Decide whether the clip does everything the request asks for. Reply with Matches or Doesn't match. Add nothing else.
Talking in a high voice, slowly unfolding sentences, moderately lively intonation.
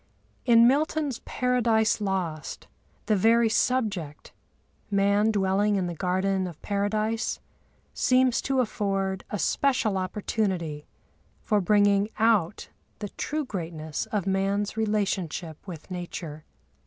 Matches